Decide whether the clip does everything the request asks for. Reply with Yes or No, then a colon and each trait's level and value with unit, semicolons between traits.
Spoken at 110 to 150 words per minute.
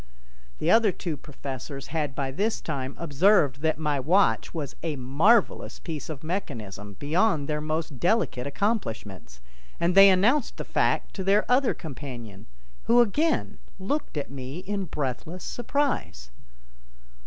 Yes: average, 140 wpm